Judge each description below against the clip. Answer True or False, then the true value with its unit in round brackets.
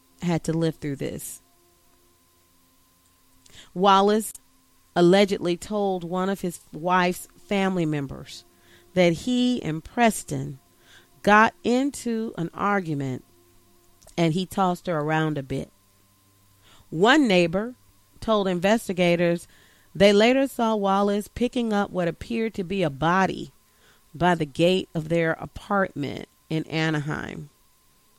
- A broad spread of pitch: True (7.0 semitones)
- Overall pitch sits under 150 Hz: False (170 Hz)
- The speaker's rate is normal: False (115 wpm)